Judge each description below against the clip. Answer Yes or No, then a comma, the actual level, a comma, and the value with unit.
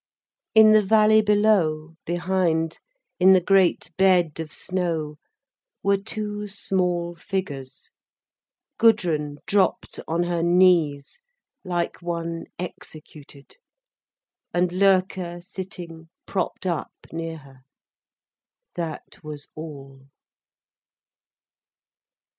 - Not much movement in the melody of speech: No, average, 3.2 semitones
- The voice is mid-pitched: Yes, medium, 175 Hz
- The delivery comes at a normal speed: No, slow, 90 wpm